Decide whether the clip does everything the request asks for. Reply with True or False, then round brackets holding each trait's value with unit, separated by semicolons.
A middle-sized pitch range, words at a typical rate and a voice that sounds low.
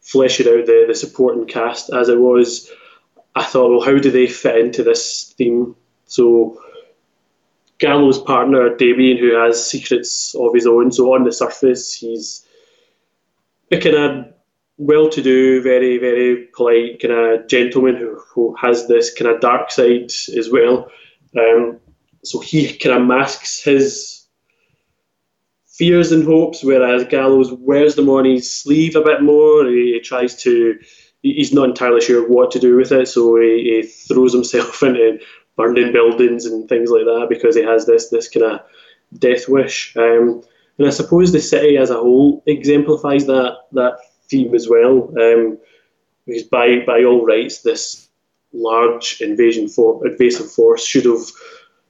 False (6.9 semitones; 160 wpm; 130 Hz)